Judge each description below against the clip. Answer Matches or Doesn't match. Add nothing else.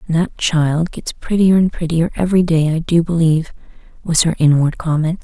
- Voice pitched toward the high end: Doesn't match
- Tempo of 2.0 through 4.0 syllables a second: Doesn't match